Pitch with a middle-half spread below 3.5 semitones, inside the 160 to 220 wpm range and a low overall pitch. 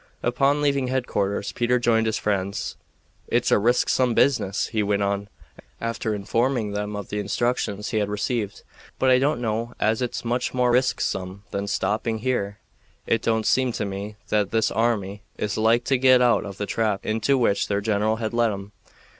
Yes: average, 3.1 semitones; average, 180 wpm; low, 110 Hz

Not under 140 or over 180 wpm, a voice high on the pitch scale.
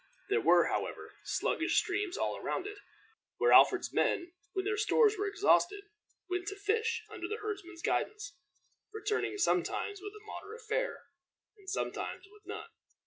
Yes: average, 150 wpm; very high, 410 Hz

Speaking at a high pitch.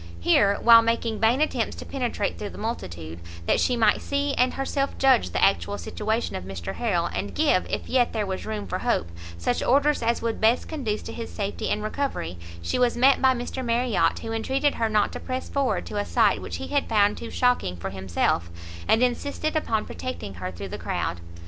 Yes: high, 225 Hz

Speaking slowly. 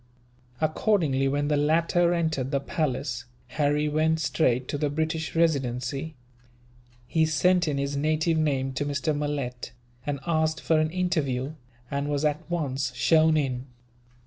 No: average, 145 wpm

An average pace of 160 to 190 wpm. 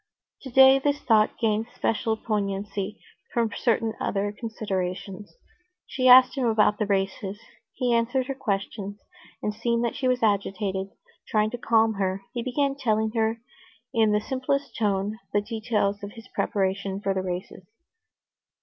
No: average, 150 wpm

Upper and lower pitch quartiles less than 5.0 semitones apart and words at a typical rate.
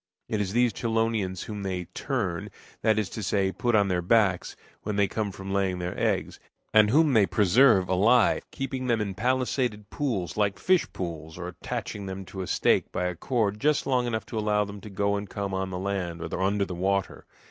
No: average, 3.1 semitones; fast, 210 wpm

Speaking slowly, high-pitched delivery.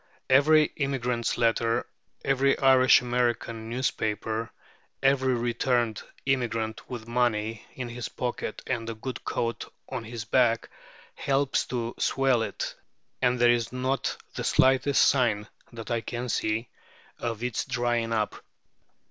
No: slow, 130 wpm; low, 120 Hz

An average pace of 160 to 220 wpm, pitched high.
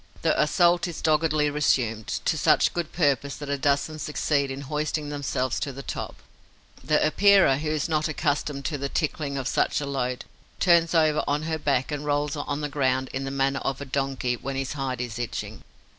No: average, 200 wpm; medium, 145 Hz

